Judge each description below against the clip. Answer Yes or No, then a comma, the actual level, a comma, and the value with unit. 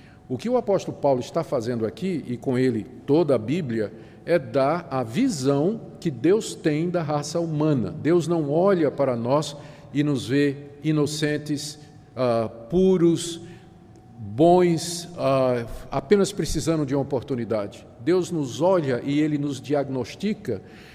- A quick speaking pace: No, average, 140 wpm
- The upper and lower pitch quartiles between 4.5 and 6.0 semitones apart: Yes, average, 4.8 semitones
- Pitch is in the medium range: Yes, medium, 145 Hz